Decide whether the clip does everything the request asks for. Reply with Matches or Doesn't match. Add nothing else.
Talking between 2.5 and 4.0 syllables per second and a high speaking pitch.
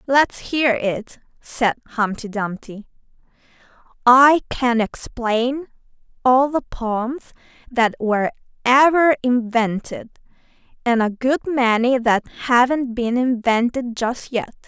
Matches